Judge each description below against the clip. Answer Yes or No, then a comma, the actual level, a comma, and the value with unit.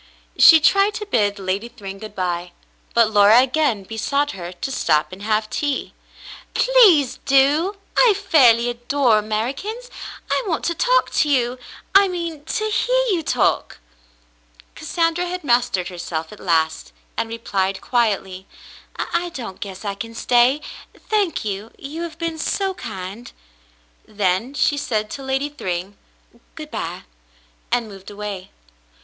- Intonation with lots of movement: Yes, wide, 7.9 semitones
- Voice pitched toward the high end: Yes, high, 240 Hz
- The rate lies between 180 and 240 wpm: No, average, 145 wpm